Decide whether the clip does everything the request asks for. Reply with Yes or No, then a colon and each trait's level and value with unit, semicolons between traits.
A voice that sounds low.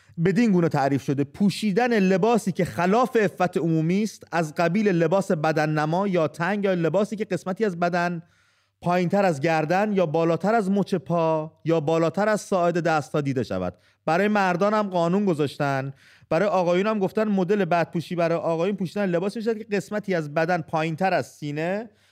No: medium, 180 Hz